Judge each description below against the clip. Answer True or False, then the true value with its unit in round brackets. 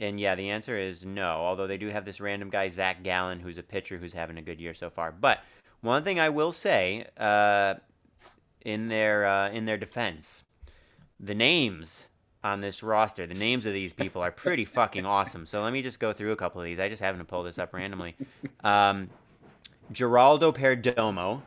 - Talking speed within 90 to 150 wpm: False (205 wpm)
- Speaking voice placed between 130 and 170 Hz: False (100 Hz)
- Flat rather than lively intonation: False (3.0 semitones)